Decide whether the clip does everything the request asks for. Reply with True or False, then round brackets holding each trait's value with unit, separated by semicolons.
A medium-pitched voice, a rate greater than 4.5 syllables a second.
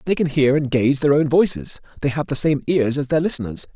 True (145 Hz; 6.0 syllables/s)